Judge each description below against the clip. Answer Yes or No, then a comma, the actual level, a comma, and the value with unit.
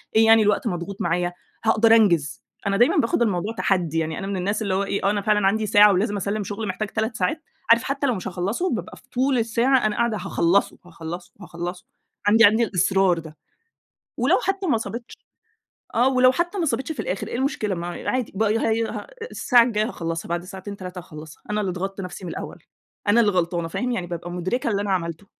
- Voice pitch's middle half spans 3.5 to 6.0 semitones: Yes, average, 4.2 semitones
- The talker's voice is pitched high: Yes, high, 200 Hz